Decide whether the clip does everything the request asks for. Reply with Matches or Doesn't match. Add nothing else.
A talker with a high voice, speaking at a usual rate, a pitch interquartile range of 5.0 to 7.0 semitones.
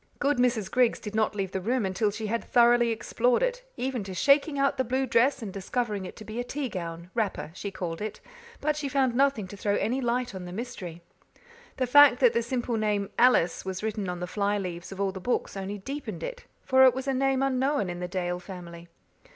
Doesn't match